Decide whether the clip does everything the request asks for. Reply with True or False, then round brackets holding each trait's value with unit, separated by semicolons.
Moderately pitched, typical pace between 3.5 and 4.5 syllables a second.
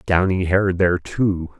False (90 Hz; 4.1 syllables/s)